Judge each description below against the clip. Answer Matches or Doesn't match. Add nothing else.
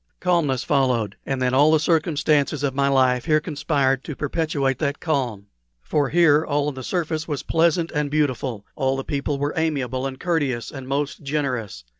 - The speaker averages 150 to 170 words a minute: Doesn't match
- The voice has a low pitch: Doesn't match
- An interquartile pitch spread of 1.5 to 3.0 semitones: Matches